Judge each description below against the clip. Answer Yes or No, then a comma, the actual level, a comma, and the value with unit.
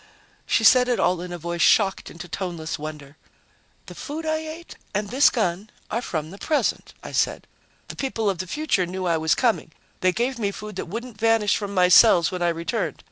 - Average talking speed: No, fast, 210 wpm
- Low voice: No, high, 195 Hz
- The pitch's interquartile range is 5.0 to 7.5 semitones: Yes, average, 5.3 semitones